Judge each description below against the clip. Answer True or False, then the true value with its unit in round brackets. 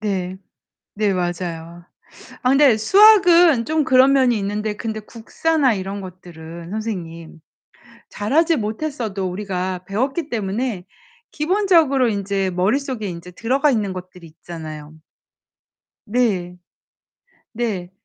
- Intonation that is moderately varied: False (6.4 semitones)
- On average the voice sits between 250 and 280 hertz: False (210 Hz)